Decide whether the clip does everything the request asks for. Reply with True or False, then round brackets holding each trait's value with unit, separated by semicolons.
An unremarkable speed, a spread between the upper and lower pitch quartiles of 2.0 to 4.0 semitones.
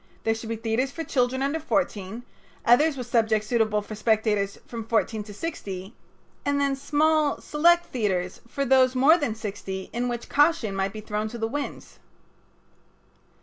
False (165 wpm; 4.6 semitones)